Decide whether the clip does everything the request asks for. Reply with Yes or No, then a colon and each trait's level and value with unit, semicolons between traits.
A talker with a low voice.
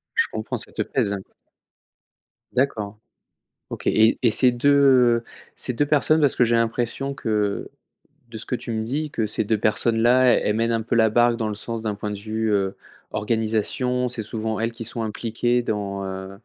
Yes: low, 115 Hz